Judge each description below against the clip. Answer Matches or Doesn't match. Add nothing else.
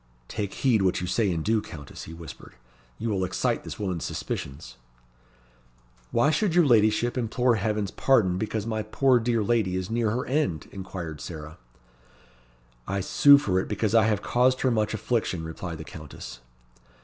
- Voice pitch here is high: Doesn't match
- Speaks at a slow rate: Doesn't match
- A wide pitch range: Doesn't match